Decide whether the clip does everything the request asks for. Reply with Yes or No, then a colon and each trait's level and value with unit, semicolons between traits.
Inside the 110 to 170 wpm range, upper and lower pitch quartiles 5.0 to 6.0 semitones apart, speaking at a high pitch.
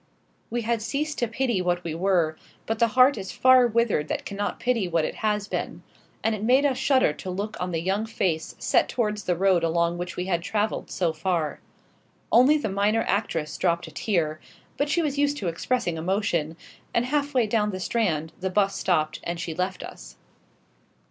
No: average, 200 wpm; wide, 5.4 semitones; high, 200 Hz